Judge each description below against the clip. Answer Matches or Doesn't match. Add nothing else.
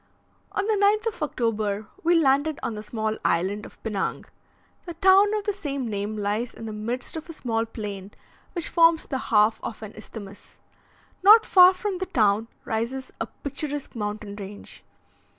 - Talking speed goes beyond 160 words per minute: Matches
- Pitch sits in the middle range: Doesn't match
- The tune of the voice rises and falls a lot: Matches